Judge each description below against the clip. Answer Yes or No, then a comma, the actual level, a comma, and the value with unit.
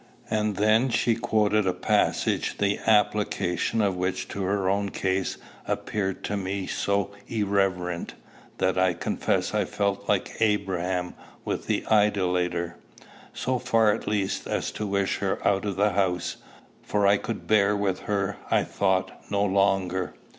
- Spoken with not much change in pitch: Yes, narrow, 1.9 semitones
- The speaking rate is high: No, average, 150 wpm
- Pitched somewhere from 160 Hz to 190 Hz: No, low, 100 Hz